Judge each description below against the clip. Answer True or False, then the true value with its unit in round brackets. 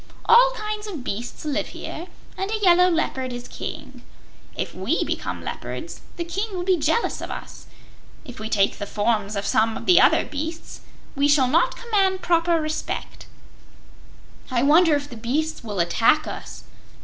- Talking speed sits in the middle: True (170 wpm)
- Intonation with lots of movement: True (7.0 semitones)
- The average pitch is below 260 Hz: False (310 Hz)